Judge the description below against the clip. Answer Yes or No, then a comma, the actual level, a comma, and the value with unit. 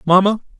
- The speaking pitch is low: No, high, 190 Hz